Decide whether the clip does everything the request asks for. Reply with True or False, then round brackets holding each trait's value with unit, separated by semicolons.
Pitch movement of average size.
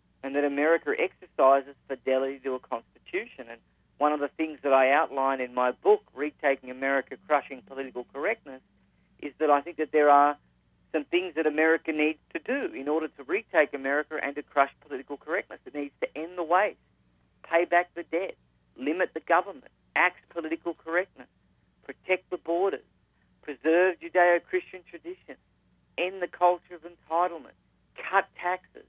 True (4.0 semitones)